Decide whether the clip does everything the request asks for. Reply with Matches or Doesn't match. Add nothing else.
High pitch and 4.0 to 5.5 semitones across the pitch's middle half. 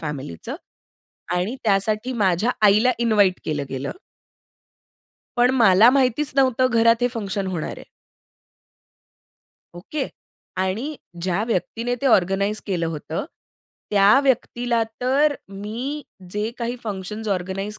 Matches